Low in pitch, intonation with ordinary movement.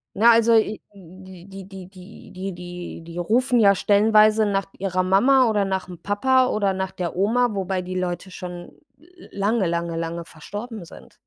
No: high, 195 Hz; average, 3.2 semitones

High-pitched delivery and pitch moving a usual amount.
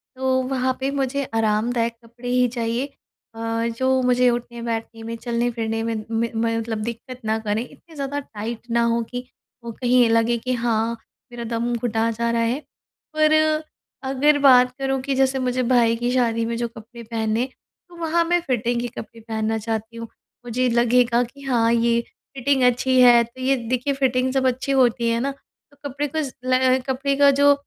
No: high, 240 Hz; narrow, 2.1 semitones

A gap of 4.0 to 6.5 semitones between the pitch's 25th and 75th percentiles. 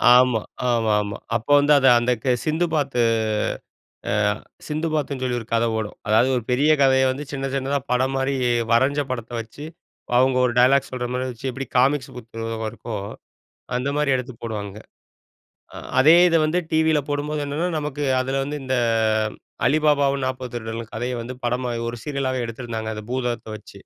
No: average, 3.2 semitones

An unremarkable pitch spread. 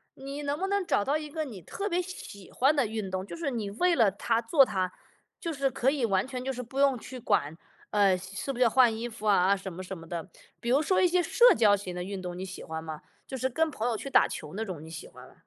No: wide, 6.5 semitones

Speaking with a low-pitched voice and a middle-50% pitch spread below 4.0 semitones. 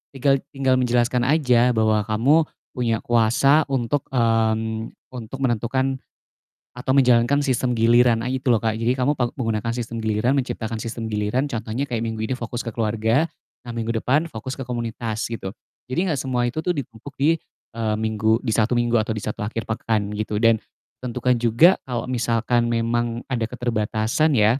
Yes: low, 120 Hz; narrow, 2.4 semitones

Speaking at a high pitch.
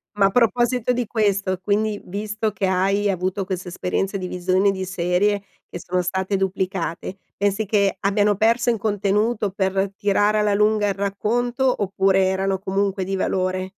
Yes: high, 195 Hz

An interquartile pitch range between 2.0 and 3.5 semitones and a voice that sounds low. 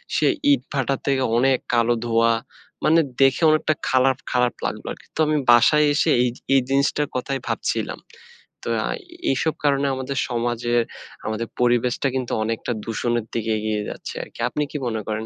Yes: average, 2.9 semitones; low, 125 Hz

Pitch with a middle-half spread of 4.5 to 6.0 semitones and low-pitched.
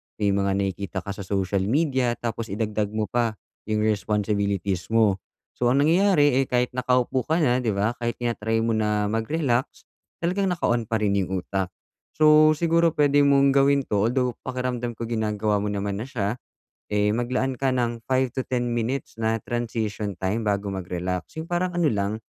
No: average, 4.1 semitones; low, 115 Hz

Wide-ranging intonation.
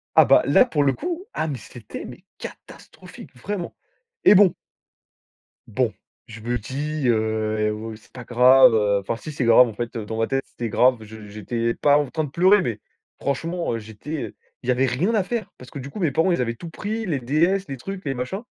Yes: wide, 6.5 semitones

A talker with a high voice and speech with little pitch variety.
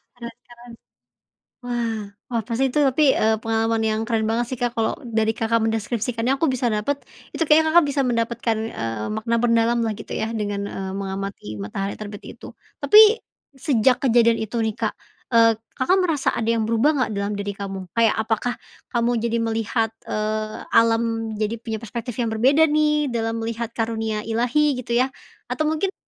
Yes: high, 230 Hz; narrow, 1.9 semitones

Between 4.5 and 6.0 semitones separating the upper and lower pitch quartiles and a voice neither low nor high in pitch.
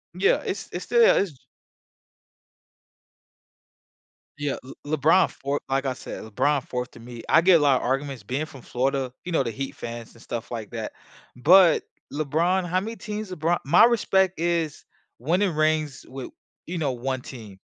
Yes: wide, 5.4 semitones; medium, 145 Hz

